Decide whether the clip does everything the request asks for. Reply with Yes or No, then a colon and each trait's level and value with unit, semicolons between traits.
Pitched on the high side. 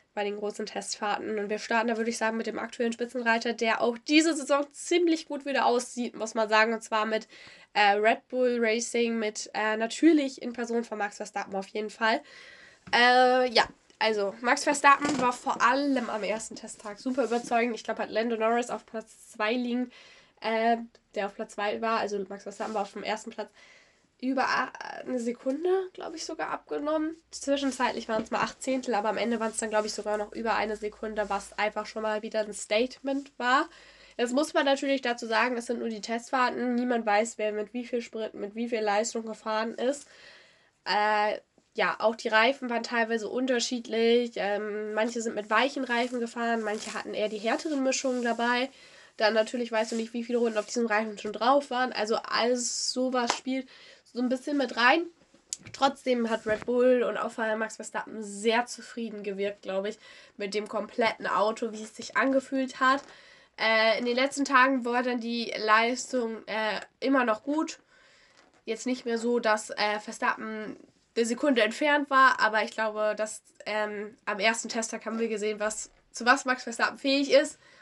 Yes: high, 230 Hz